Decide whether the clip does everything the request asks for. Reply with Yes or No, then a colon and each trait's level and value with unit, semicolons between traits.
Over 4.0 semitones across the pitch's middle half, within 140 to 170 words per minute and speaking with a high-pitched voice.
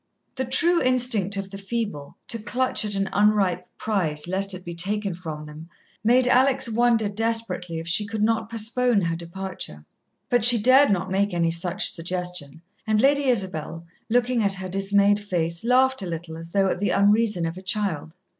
No: average, 4.6 semitones; average, 185 wpm; high, 200 Hz